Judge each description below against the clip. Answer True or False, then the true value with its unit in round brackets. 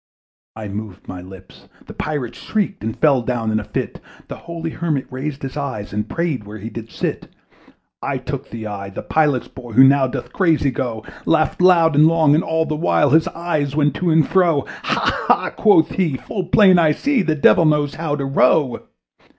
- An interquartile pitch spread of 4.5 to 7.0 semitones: True (5.2 semitones)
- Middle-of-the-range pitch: True (145 Hz)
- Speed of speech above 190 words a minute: True (200 wpm)